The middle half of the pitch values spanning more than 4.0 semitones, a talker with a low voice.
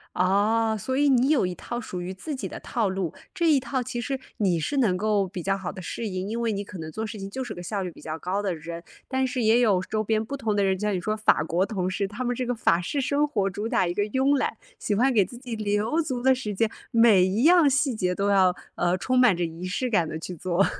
No: average, 5.0 semitones; high, 210 Hz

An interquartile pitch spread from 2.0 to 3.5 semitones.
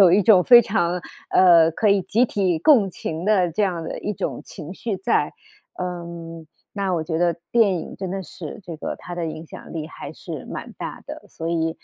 Yes: average, 3.1 semitones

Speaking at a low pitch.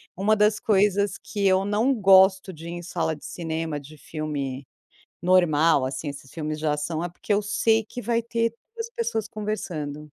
No: medium, 185 Hz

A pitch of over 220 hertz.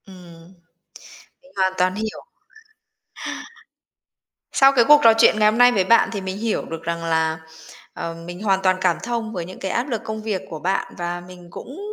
No: high, 190 Hz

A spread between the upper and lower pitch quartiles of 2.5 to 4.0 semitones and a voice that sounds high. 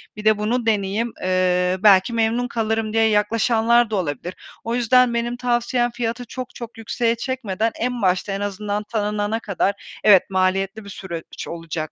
Yes: average, 3.3 semitones; high, 215 Hz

